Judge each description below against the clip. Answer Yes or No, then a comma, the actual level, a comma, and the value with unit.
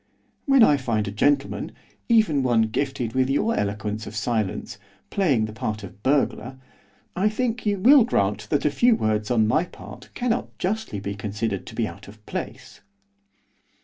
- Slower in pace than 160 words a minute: No, average, 170 wpm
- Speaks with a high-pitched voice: No, low, 125 Hz